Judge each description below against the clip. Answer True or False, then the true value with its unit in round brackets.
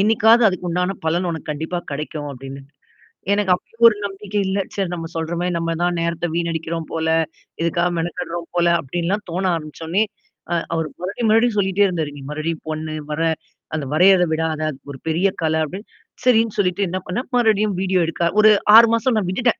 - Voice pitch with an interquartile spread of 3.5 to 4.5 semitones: True (3.8 semitones)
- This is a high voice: False (175 Hz)